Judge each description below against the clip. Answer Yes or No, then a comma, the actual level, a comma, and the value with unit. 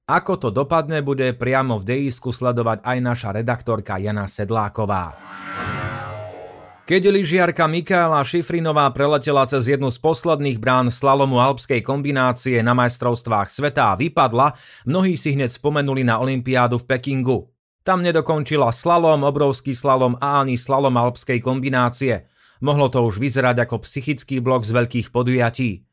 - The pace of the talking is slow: No, average, 135 wpm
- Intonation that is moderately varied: Yes, average, 3.1 semitones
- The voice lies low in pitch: Yes, low, 130 Hz